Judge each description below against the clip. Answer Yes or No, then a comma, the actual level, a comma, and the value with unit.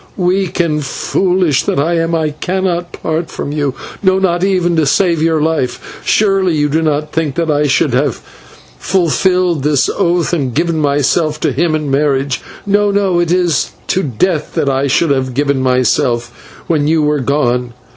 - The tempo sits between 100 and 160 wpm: No, average, 175 wpm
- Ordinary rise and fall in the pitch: Yes, average, 3.7 semitones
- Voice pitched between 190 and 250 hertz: No, medium, 155 Hz